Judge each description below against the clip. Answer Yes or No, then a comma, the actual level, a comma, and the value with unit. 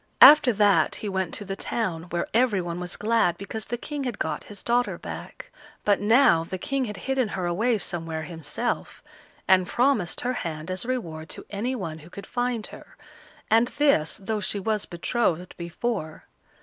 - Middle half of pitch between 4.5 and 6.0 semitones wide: Yes, wide, 5.6 semitones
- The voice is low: No, high, 200 Hz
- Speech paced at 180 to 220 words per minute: Yes, average, 185 wpm